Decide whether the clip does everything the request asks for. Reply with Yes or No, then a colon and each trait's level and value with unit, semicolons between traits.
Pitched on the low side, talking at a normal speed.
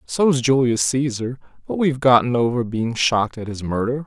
Yes: low, 125 Hz; average, 175 wpm